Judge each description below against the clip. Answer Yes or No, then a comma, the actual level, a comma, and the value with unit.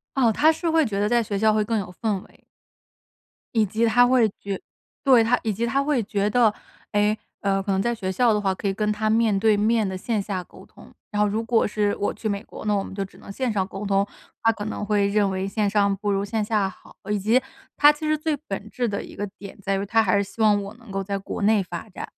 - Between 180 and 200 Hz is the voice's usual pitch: No, high, 210 Hz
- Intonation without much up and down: Yes, narrow, 2.3 semitones